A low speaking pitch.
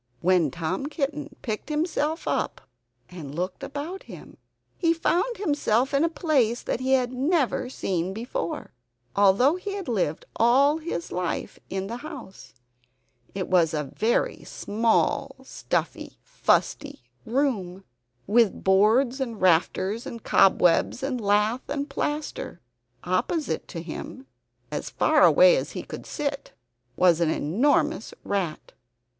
No: high, 240 Hz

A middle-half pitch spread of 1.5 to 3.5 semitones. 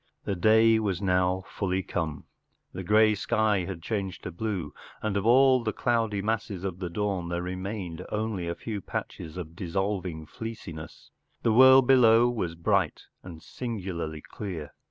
No: average, 4.1 semitones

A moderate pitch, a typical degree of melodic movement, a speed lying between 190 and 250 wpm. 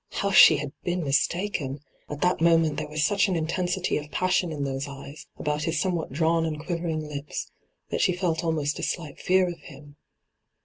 Yes: medium, 160 Hz; average, 3.1 semitones; average, 195 wpm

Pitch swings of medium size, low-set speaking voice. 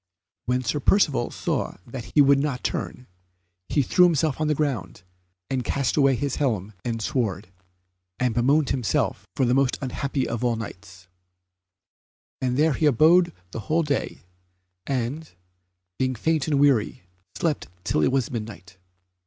Yes: average, 3.8 semitones; low, 130 Hz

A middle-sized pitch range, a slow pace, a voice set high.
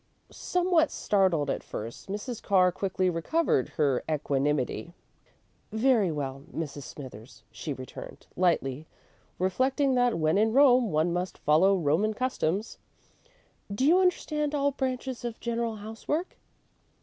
No: wide, 8.6 semitones; slow, 125 wpm; high, 195 Hz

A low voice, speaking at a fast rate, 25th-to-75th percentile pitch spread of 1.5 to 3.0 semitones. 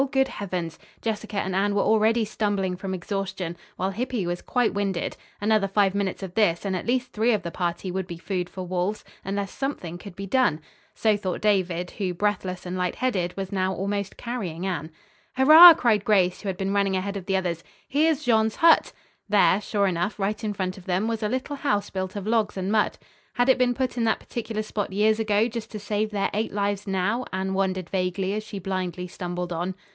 No: high, 200 Hz; fast, 210 wpm; average, 2.7 semitones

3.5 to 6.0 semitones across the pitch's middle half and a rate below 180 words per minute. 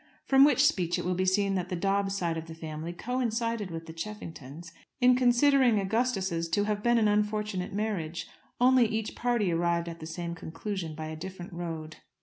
No: average, 4.8 semitones; average, 190 wpm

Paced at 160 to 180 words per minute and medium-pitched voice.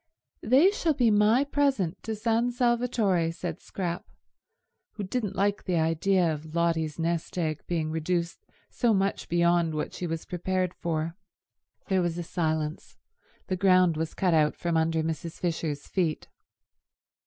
No: average, 145 wpm; medium, 175 Hz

